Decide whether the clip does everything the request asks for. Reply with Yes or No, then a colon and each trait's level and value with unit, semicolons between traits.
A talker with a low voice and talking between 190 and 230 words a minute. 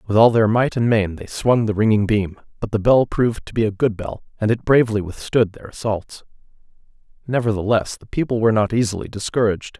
Yes: low, 110 Hz; average, 200 wpm